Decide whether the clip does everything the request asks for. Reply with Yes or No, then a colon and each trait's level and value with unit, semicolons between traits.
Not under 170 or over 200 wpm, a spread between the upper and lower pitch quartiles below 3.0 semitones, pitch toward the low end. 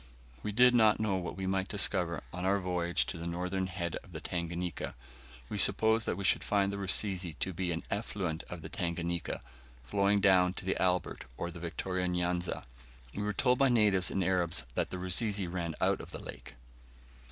Yes: average, 195 wpm; narrow, 2.4 semitones; very low, 90 Hz